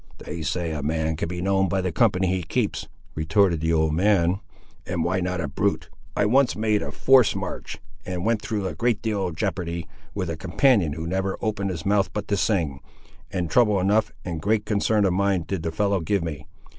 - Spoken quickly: Yes, fast, 210 wpm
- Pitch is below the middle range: Yes, very low, 95 Hz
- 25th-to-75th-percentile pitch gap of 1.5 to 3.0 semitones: No, average, 3.7 semitones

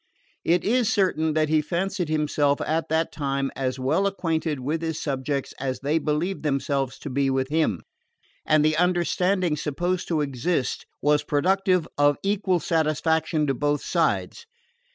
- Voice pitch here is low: No, medium, 155 Hz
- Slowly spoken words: No, average, 155 wpm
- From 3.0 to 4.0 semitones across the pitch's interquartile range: Yes, average, 3.6 semitones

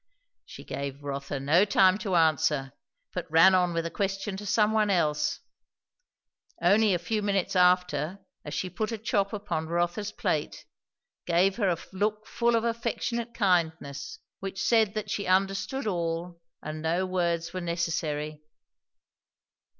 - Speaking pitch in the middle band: Yes, medium, 180 Hz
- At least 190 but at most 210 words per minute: No, average, 150 wpm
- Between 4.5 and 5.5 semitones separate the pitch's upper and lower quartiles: No, average, 3.8 semitones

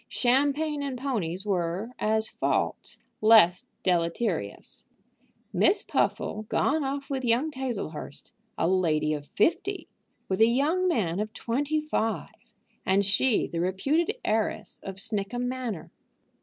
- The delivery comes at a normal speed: No, slow, 125 wpm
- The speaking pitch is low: No, high, 225 Hz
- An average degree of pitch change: No, wide, 6.4 semitones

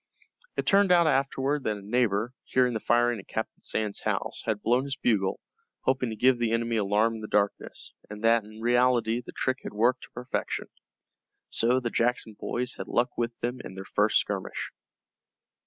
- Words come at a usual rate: Yes, average, 190 wpm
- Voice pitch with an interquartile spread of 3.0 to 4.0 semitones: No, narrow, 2.6 semitones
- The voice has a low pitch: Yes, low, 120 Hz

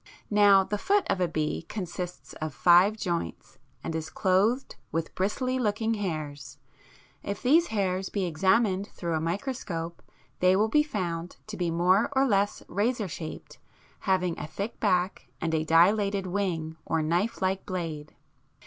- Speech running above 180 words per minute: No, average, 160 wpm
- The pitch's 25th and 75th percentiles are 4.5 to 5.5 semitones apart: No, average, 3.8 semitones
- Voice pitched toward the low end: No, medium, 185 Hz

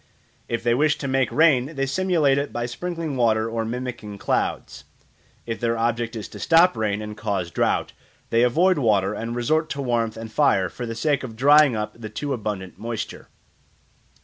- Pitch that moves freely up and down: No, average, 4.1 semitones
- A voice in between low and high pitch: No, low, 120 Hz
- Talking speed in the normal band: Yes, average, 185 wpm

